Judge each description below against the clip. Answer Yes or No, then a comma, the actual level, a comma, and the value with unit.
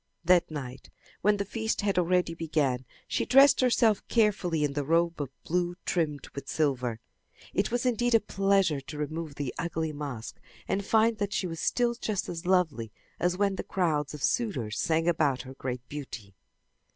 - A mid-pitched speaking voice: Yes, medium, 165 Hz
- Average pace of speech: Yes, average, 175 wpm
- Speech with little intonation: No, wide, 5.5 semitones